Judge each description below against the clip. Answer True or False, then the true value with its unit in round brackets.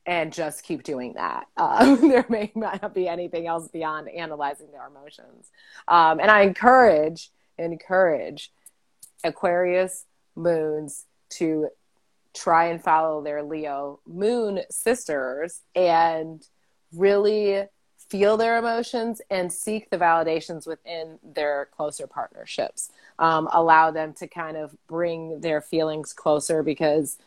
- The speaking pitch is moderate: True (165 Hz)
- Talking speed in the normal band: False (120 wpm)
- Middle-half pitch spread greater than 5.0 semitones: False (3.5 semitones)